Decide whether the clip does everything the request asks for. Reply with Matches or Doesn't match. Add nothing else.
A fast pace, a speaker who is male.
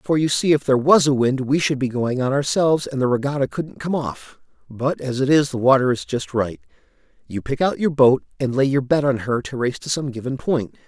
Matches